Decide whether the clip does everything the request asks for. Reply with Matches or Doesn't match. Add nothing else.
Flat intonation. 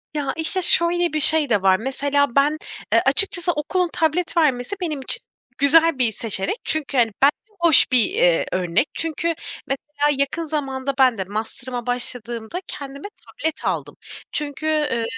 Doesn't match